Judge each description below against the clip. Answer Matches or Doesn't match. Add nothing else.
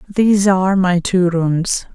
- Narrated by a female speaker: Matches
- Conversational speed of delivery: Matches